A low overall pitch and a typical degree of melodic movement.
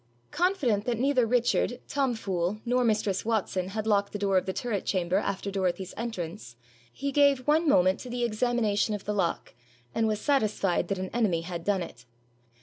No: high, 210 Hz; average, 4.4 semitones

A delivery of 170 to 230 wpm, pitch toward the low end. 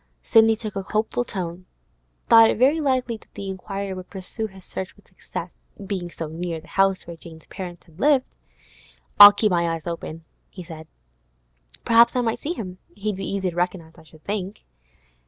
No: average, 185 wpm; high, 190 Hz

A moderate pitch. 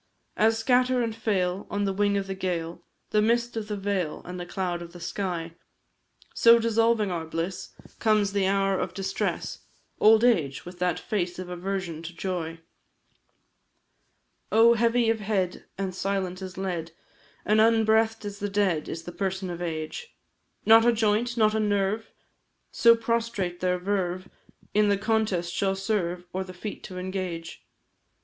No: high, 195 Hz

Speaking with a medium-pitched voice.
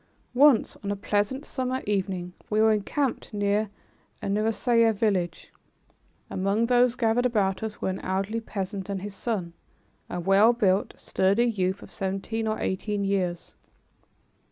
No: high, 205 Hz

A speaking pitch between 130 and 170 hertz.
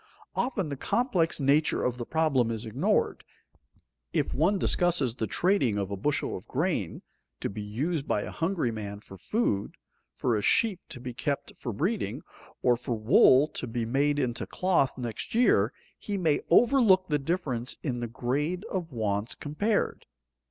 Yes: medium, 140 Hz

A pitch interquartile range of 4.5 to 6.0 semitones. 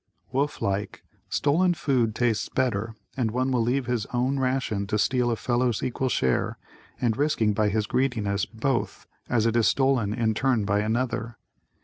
No: average, 3.2 semitones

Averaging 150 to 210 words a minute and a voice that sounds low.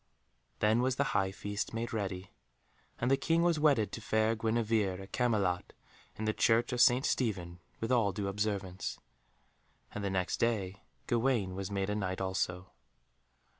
Yes: average, 165 wpm; low, 105 Hz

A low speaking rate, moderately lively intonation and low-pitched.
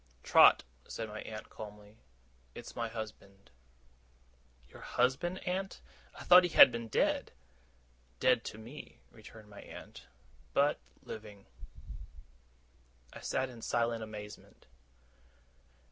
Yes: slow, 115 wpm; average, 3.3 semitones; low, 115 Hz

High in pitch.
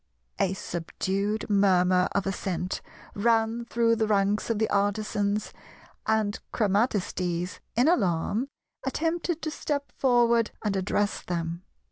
Yes: high, 205 Hz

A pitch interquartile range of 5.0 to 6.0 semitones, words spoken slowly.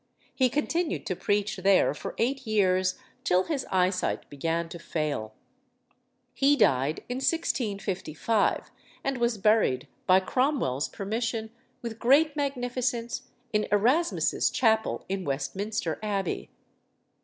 Yes: average, 5.3 semitones; slow, 115 wpm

